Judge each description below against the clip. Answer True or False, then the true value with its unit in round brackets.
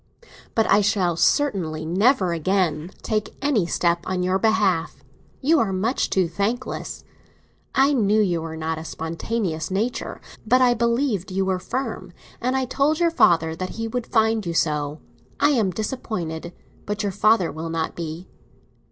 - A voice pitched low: False (195 Hz)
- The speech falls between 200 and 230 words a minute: False (160 wpm)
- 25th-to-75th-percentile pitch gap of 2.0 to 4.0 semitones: False (5.5 semitones)